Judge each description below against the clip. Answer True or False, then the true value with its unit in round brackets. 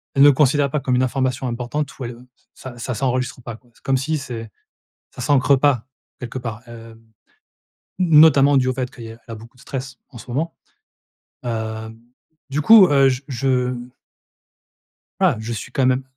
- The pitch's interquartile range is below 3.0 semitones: True (2.6 semitones)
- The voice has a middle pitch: False (130 Hz)